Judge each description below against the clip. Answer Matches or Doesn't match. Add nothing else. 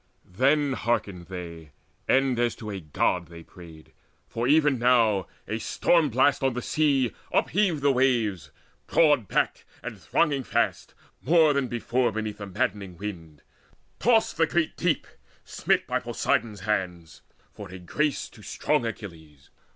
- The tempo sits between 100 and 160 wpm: Matches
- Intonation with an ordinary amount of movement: Doesn't match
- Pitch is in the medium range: Doesn't match